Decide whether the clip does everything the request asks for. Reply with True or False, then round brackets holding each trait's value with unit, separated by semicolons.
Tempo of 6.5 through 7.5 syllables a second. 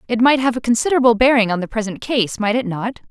True (6.7 syllables/s)